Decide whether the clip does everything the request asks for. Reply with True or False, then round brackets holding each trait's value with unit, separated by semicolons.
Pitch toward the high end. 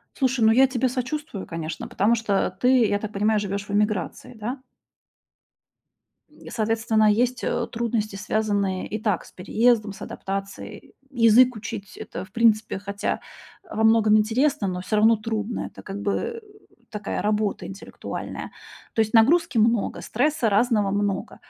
True (215 Hz)